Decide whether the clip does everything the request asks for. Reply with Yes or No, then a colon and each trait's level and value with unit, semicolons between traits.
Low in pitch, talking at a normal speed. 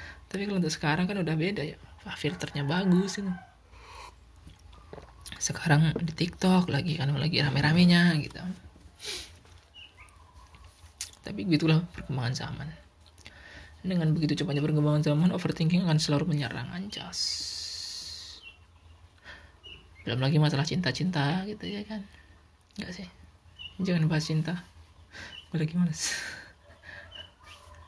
No: medium, 145 Hz; average, 110 wpm